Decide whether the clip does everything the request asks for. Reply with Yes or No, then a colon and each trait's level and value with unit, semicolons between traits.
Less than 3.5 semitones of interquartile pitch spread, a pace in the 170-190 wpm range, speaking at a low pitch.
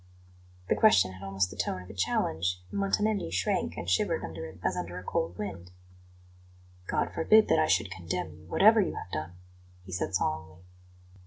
Yes: narrow, 2.6 semitones; average, 185 wpm; very low, 90 Hz